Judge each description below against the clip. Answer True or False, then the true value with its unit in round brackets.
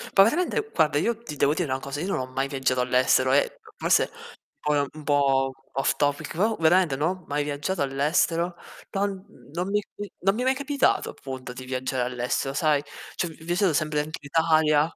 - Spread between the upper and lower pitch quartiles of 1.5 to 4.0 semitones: False (5.0 semitones)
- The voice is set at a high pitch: False (150 Hz)